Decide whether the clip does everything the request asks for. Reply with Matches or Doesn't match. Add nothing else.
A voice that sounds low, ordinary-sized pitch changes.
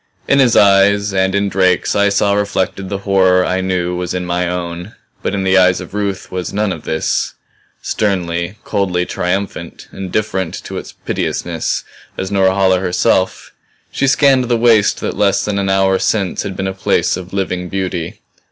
Doesn't match